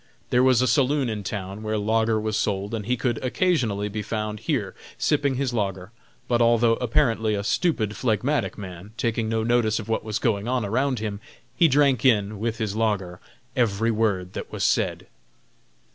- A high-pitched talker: No, low, 110 Hz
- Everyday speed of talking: Yes, average, 180 wpm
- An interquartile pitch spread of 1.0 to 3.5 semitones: Yes, average, 3.0 semitones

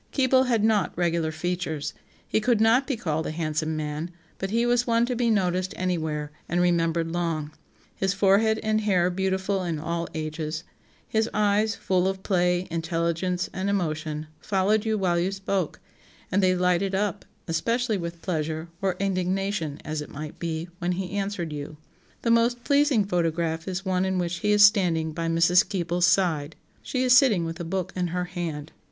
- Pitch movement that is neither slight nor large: Yes, average, 3.5 semitones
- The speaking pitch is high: No, medium, 180 Hz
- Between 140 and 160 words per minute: No, average, 180 wpm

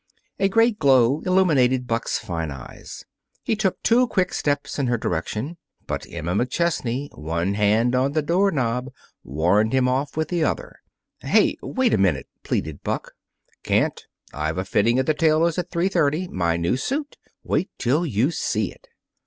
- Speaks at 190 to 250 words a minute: No, average, 170 wpm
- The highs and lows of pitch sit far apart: Yes, wide, 8.5 semitones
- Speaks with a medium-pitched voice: No, low, 130 Hz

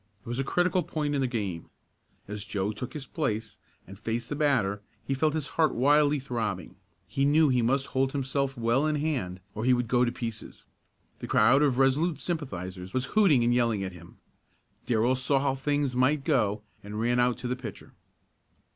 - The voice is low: Yes, low, 125 Hz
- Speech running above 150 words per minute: Yes, average, 195 wpm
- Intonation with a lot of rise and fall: No, average, 4.5 semitones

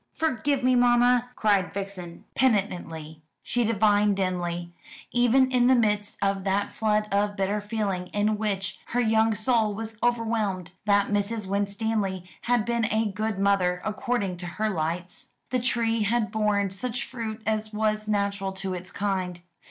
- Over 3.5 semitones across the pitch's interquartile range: No, narrow, 2.6 semitones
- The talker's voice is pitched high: Yes, high, 210 Hz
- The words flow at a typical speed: Yes, average, 150 wpm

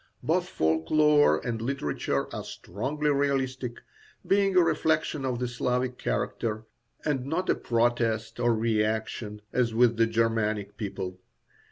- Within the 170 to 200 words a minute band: No, slow, 135 wpm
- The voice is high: No, low, 120 Hz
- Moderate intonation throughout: Yes, average, 4.0 semitones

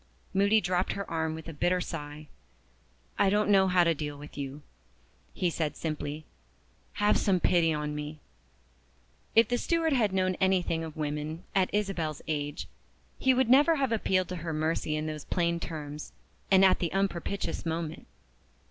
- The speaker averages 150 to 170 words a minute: Yes, average, 165 wpm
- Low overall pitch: No, medium, 170 Hz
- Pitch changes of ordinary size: Yes, average, 4.1 semitones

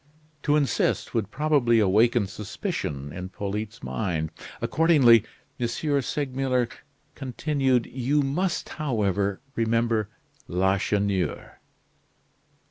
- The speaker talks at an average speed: No, slow, 85 wpm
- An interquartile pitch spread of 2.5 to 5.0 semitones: No, wide, 5.4 semitones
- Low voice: Yes, low, 115 Hz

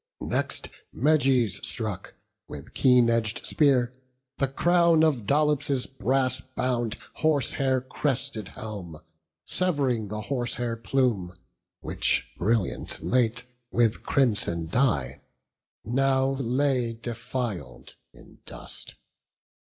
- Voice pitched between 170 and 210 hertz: No, low, 125 Hz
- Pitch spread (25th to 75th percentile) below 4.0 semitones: Yes, average, 3.4 semitones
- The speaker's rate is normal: No, slow, 95 wpm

